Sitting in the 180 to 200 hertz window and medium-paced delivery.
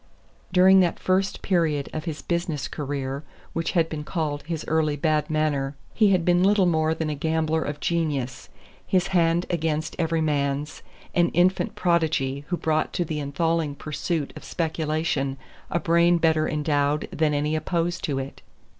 No: medium, 160 Hz; average, 165 wpm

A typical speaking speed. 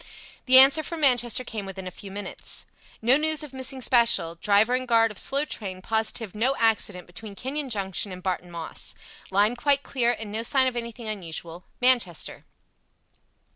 Yes: average, 175 wpm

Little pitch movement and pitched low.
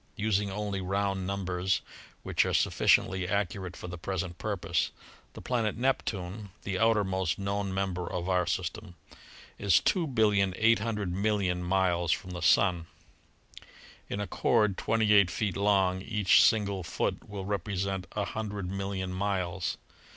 Yes: narrow, 2.1 semitones; very low, 95 Hz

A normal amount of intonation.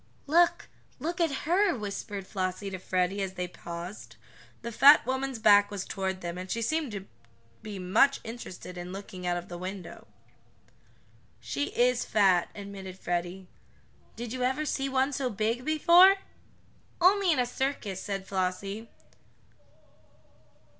No: wide, 6.1 semitones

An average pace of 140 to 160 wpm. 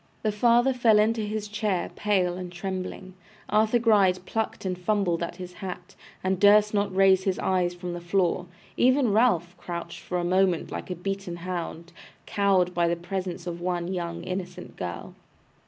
No: average, 170 wpm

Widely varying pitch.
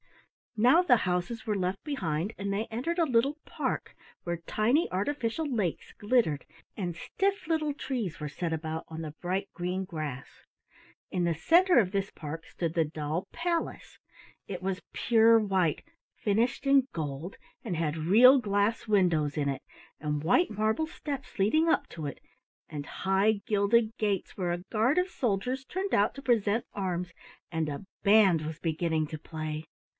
Yes: wide, 6.5 semitones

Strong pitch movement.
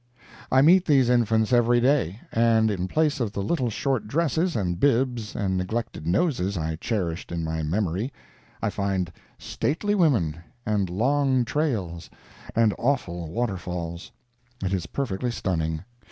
Yes: wide, 6.5 semitones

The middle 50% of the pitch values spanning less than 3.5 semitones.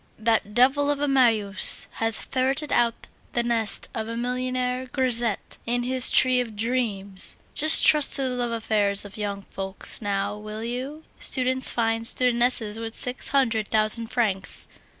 Yes: average, 2.9 semitones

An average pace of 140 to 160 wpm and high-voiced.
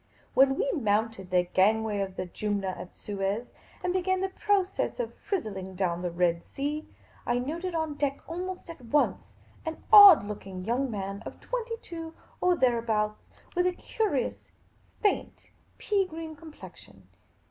Yes: average, 155 wpm; very high, 270 Hz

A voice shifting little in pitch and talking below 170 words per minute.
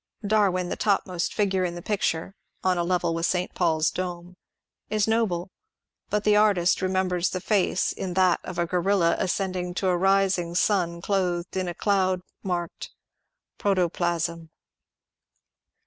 Yes: narrow, 1.9 semitones; average, 150 wpm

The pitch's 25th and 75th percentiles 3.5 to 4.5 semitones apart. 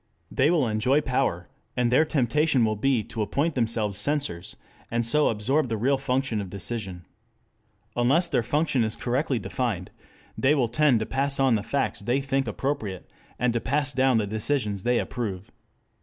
Yes: average, 4.1 semitones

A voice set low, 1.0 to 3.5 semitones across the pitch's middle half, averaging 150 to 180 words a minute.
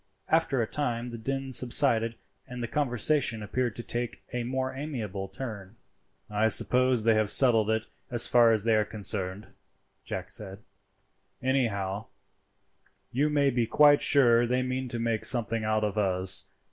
Yes: low, 115 Hz; average, 3.0 semitones; average, 160 wpm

